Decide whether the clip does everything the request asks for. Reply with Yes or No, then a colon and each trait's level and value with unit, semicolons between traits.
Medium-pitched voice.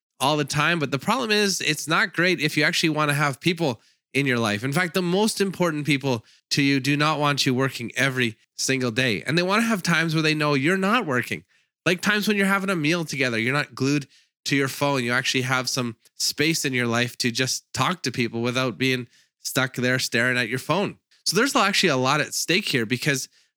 Yes: medium, 145 Hz